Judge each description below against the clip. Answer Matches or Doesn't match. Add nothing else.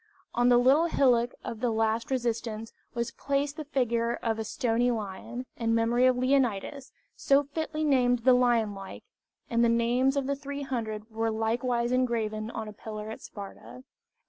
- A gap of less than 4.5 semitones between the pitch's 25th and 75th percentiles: Matches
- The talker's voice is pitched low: Doesn't match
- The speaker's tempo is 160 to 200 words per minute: Matches